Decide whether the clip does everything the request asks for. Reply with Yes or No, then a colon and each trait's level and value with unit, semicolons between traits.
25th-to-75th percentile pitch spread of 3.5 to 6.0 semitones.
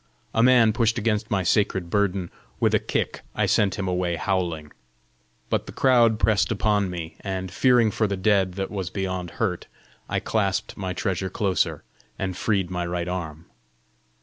No: average, 3.0 semitones